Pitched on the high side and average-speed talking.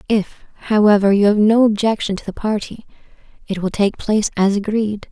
Yes: high, 210 Hz; average, 175 wpm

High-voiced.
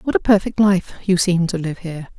No: medium, 180 Hz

